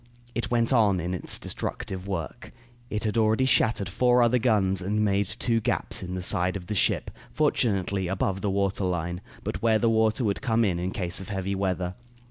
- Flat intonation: No, average, 3.3 semitones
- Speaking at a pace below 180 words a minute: No, average, 200 wpm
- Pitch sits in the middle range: No, low, 100 Hz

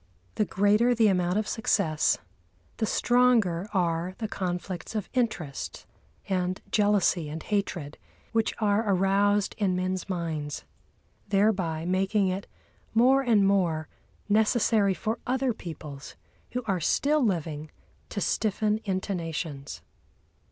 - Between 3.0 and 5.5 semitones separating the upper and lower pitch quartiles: Yes, average, 3.8 semitones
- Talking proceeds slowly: Yes, slow, 120 wpm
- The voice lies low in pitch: No, high, 195 Hz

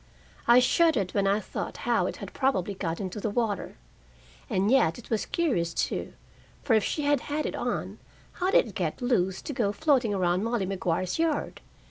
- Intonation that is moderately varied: No, wide, 6.1 semitones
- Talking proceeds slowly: No, average, 190 wpm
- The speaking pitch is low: No, high, 215 Hz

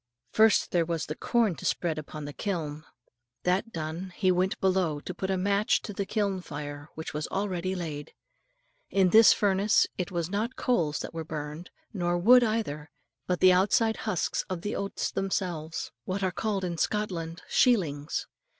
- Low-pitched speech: No, medium, 180 Hz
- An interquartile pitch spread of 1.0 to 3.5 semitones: No, average, 3.9 semitones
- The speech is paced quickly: No, average, 175 wpm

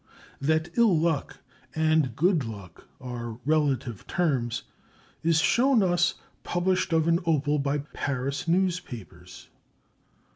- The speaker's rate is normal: No, slow, 110 wpm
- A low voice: No, medium, 155 Hz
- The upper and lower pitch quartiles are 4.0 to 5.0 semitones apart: Yes, average, 4.7 semitones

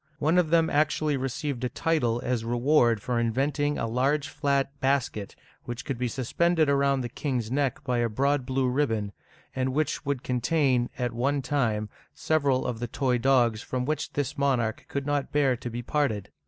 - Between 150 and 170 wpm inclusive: No, average, 180 wpm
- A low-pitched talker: Yes, low, 130 Hz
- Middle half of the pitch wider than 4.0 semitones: No, average, 3.1 semitones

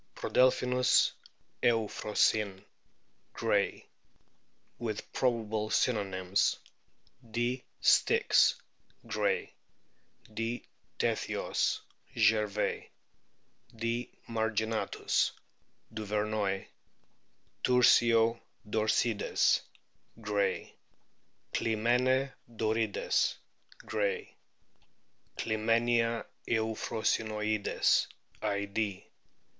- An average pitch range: No, narrow, 1.7 semitones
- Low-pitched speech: Yes, low, 110 Hz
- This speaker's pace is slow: Yes, slow, 50 wpm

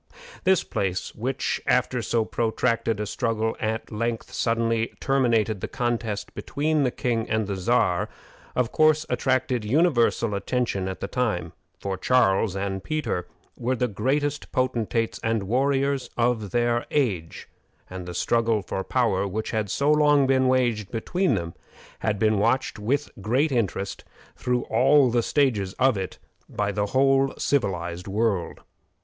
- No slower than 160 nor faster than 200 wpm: No, average, 145 wpm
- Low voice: Yes, low, 115 Hz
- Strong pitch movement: No, average, 4.1 semitones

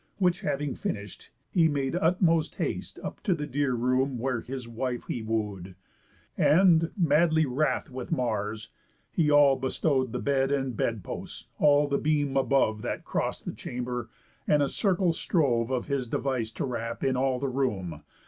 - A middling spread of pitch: Yes, average, 3.6 semitones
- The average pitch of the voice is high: No, low, 135 Hz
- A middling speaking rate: Yes, average, 165 wpm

